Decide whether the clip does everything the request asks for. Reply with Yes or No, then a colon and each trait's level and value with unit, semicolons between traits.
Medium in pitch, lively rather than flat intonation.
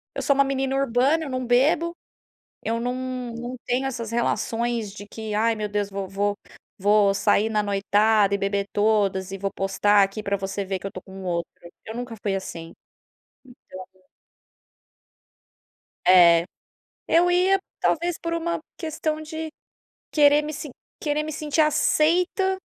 No: high, 230 Hz; wide, 6.6 semitones